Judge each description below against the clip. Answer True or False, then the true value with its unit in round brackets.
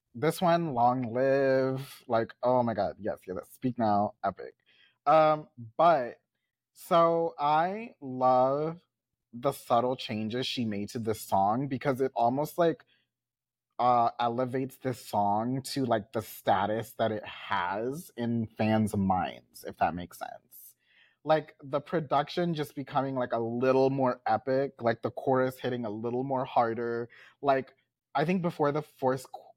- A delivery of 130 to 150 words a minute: True (145 wpm)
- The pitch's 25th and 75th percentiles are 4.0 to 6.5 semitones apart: False (3.3 semitones)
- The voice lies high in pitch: False (130 Hz)